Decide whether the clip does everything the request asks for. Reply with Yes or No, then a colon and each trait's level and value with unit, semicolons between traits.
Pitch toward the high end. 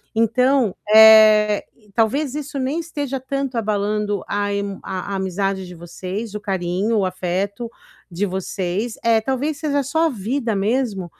Yes: high, 215 Hz